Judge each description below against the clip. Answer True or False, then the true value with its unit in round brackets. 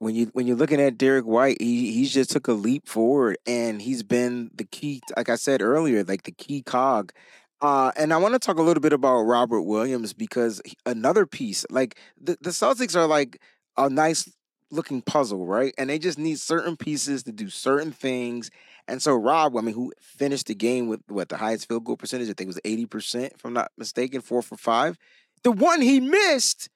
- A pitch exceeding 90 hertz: True (135 Hz)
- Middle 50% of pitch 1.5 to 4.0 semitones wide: False (5.3 semitones)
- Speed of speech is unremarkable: False (220 wpm)